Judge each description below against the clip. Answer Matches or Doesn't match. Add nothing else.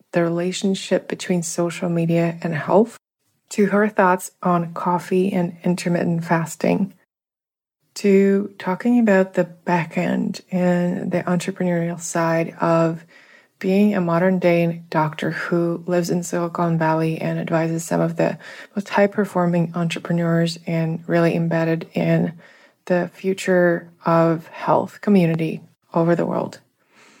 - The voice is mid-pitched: Matches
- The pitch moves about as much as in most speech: Doesn't match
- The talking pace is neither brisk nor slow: Doesn't match